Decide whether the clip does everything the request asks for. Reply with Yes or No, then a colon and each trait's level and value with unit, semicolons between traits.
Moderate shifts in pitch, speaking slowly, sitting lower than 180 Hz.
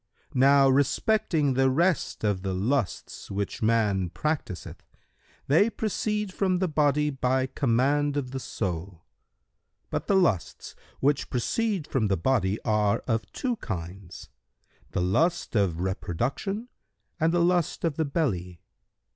No: wide, 8.3 semitones; slow, 130 wpm; low, 135 Hz